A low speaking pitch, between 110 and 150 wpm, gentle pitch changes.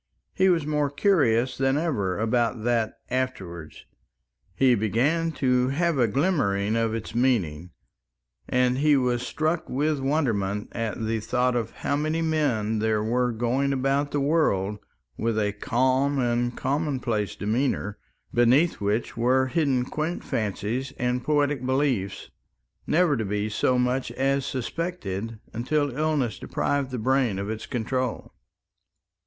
No: low, 125 Hz; slow, 135 wpm; average, 4.3 semitones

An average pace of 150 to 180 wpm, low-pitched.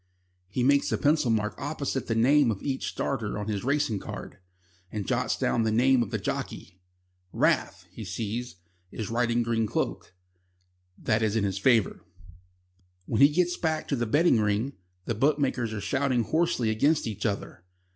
Yes: average, 170 wpm; low, 120 Hz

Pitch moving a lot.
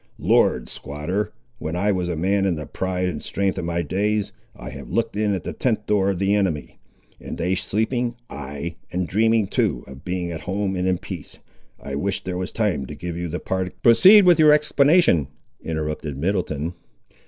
No: average, 3.7 semitones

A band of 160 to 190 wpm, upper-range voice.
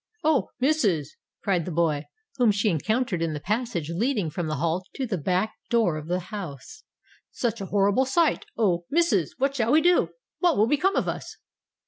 Yes: average, 175 wpm; high, 205 Hz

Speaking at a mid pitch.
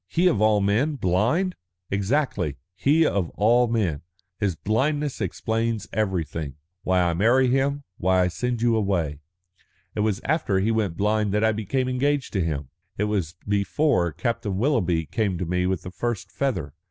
No: low, 105 Hz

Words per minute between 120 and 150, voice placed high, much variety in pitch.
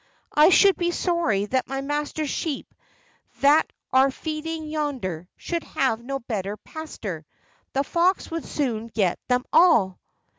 Yes: average, 140 wpm; very high, 275 Hz; wide, 5.9 semitones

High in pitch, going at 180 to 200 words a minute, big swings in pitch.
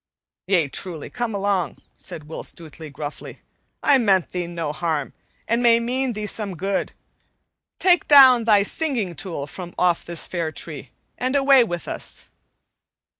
No: high, 195 Hz; average, 150 wpm; wide, 6.1 semitones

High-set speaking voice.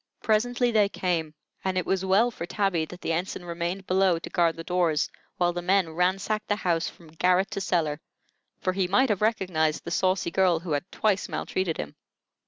No: medium, 180 Hz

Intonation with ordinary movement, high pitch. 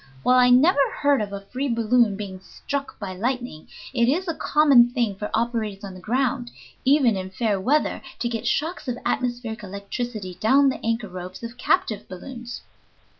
Yes: average, 4.2 semitones; high, 235 Hz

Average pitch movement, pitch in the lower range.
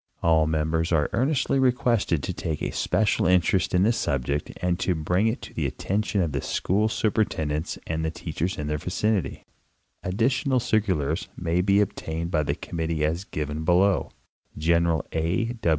Yes: average, 4.8 semitones; very low, 85 Hz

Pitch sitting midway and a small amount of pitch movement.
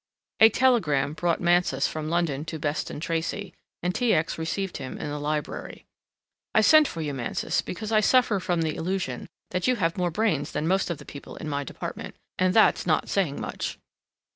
No: medium, 170 Hz; average, 4.6 semitones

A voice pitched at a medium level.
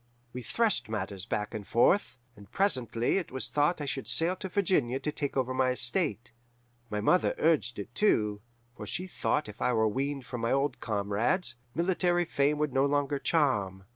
No: low, 130 Hz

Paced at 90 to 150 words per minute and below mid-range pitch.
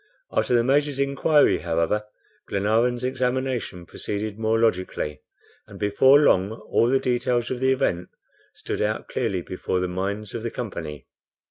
Yes: average, 145 wpm; low, 115 Hz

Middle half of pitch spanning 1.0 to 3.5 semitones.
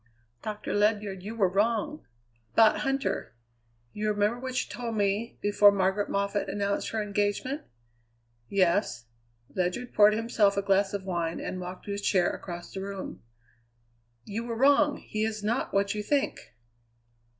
Yes: narrow, 2.4 semitones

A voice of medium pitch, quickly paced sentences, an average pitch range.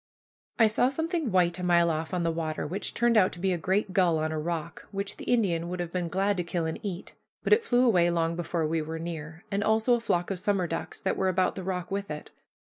Yes: medium, 180 Hz; fast, 260 wpm; average, 3.2 semitones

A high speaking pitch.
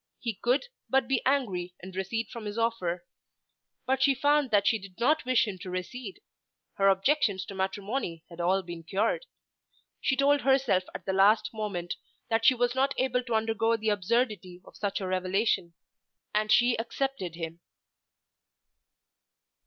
Yes: high, 215 Hz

